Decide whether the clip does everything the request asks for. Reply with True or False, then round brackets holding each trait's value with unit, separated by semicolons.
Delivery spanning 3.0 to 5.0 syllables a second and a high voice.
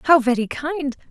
True (4.8 syllables/s; 280 Hz)